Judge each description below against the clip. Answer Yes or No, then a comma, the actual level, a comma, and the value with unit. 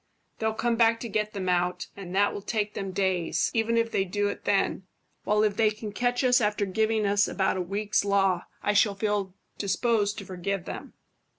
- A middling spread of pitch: No, narrow, 2.2 semitones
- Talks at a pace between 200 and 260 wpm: Yes, fast, 205 wpm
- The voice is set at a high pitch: Yes, high, 205 Hz